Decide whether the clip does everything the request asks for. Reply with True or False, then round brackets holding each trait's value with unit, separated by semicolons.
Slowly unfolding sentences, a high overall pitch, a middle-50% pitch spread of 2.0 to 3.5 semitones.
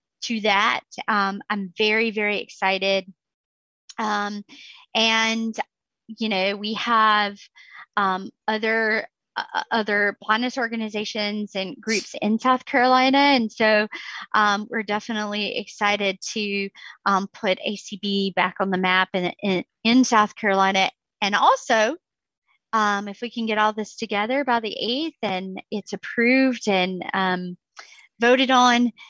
True (130 wpm; 215 Hz; 2.5 semitones)